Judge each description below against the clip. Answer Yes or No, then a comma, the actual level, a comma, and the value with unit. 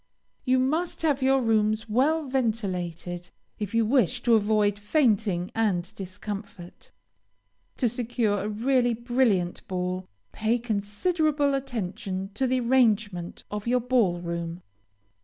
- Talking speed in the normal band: No, slow, 120 wpm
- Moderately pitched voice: No, high, 220 Hz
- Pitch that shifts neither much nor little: Yes, average, 4.6 semitones